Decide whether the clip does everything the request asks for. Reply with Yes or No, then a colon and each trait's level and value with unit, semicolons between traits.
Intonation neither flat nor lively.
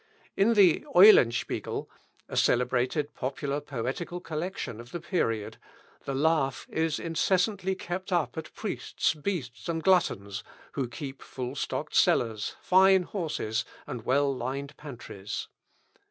No: wide, 6.0 semitones